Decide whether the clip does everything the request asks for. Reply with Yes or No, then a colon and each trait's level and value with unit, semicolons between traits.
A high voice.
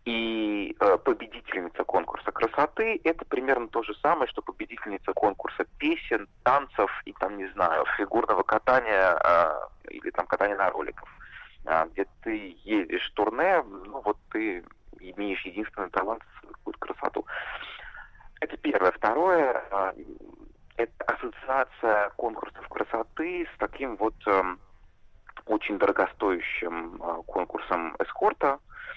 Yes: very high, 315 Hz